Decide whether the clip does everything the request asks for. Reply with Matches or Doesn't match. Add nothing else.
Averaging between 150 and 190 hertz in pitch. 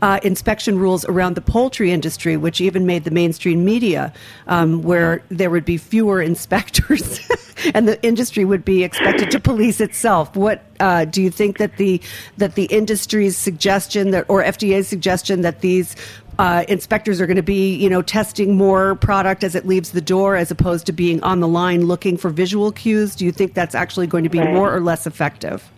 Matches